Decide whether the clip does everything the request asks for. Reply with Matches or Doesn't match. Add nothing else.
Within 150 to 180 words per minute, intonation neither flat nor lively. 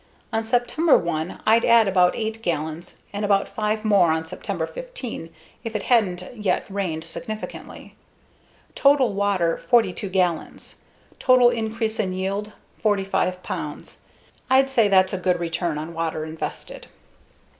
Doesn't match